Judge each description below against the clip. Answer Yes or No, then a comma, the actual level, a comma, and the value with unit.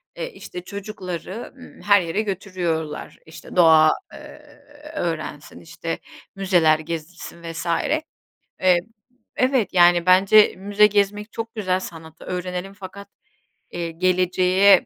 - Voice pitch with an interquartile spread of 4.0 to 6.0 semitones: No, average, 3.1 semitones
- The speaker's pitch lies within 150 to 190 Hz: Yes, medium, 185 Hz